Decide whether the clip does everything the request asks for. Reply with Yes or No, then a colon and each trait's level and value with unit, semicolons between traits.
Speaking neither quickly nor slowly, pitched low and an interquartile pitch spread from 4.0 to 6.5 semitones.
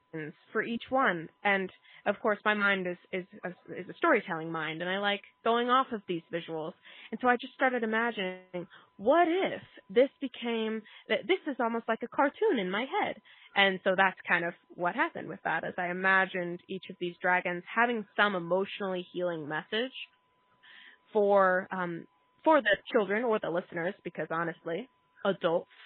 No: average, 170 wpm; high, 195 Hz; average, 4.7 semitones